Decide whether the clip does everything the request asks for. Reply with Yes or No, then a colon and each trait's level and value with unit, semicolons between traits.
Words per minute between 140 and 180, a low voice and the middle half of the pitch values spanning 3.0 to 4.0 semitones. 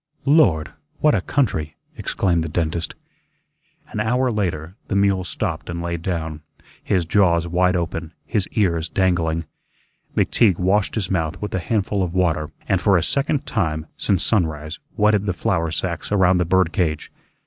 Yes: average, 160 wpm; very low, 90 Hz; average, 3.5 semitones